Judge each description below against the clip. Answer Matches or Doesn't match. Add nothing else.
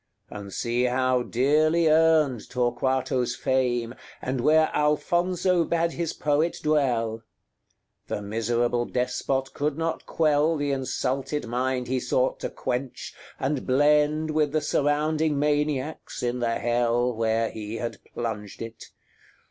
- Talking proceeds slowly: Matches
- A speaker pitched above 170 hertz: Doesn't match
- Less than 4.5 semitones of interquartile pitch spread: Matches